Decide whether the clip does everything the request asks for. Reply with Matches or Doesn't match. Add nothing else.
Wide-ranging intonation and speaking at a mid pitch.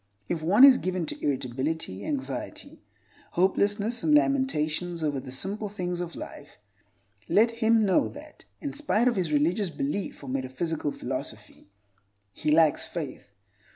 Matches